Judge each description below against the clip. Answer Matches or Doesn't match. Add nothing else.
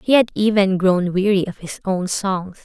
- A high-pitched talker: Matches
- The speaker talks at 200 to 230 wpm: Matches